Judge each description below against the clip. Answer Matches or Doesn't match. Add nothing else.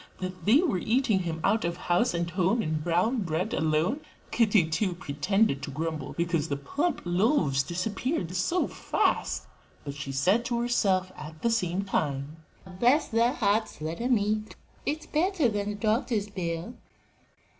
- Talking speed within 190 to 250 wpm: Doesn't match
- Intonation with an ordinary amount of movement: Doesn't match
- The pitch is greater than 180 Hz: Matches